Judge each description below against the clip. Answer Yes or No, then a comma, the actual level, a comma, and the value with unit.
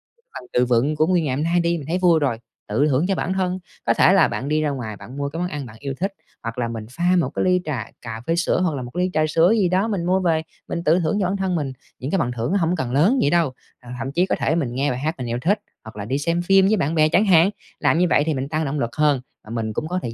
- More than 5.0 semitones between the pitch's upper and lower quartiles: Yes, wide, 5.4 semitones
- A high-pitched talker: No, medium, 155 Hz